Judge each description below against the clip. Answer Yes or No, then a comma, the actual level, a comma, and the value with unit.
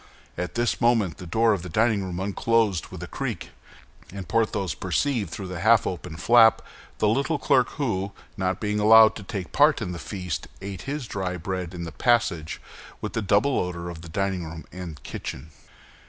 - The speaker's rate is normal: Yes, average, 190 wpm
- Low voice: Yes, low, 100 Hz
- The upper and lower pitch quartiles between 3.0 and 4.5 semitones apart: Yes, average, 4.1 semitones